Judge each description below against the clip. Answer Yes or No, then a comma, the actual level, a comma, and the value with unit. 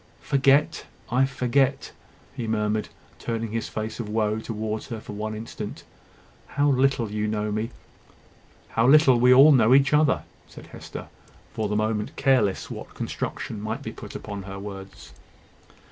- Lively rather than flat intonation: No, average, 3.5 semitones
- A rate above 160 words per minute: No, average, 155 wpm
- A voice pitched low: Yes, low, 110 Hz